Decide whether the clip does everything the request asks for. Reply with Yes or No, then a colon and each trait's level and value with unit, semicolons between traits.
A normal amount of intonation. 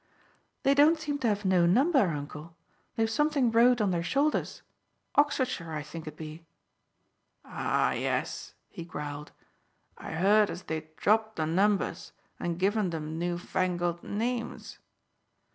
No: wide, 6.2 semitones